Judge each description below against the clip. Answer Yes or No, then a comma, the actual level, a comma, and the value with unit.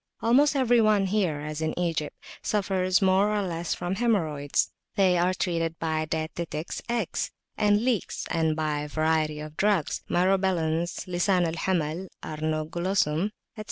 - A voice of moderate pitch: Yes, medium, 175 Hz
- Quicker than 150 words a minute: No, average, 145 wpm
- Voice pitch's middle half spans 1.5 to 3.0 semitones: No, average, 3.7 semitones